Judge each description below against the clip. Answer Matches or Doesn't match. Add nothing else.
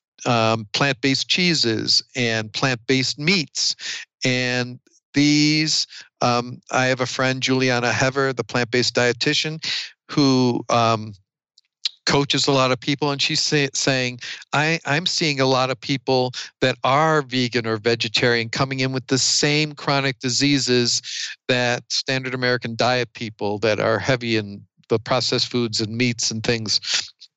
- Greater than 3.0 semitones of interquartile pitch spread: Doesn't match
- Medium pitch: Doesn't match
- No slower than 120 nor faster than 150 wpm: Matches